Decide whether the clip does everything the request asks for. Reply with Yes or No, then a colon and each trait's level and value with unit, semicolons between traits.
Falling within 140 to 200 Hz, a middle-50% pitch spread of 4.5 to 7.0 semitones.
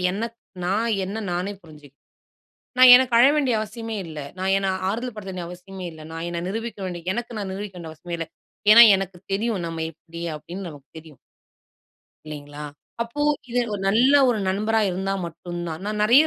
Yes: high, 190 Hz; average, 4.8 semitones